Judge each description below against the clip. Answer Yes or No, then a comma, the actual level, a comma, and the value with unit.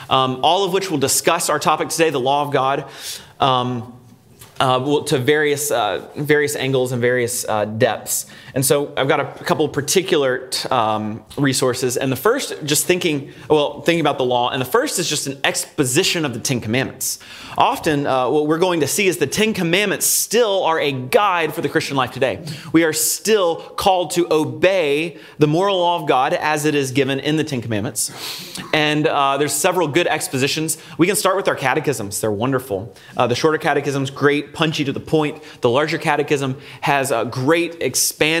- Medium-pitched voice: Yes, medium, 150 Hz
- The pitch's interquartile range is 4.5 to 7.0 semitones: No, average, 3.8 semitones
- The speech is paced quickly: No, average, 195 wpm